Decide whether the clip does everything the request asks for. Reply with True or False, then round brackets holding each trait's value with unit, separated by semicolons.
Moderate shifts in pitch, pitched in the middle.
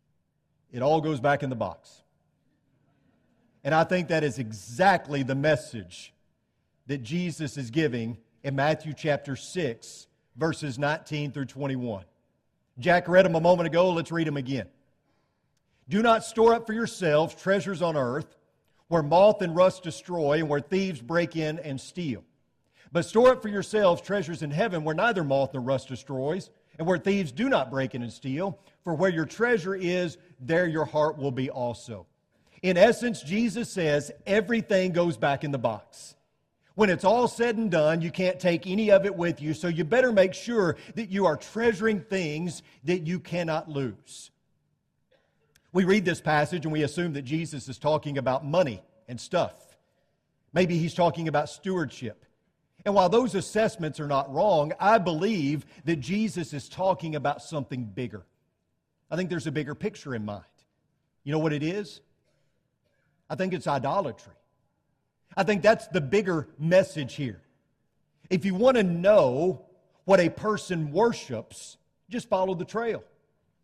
True (4.9 semitones; 160 Hz)